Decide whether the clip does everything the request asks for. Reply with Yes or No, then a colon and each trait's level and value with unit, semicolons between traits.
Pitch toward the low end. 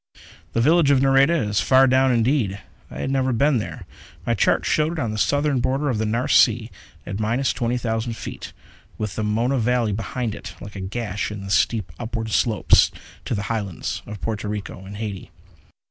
Yes: low, 115 Hz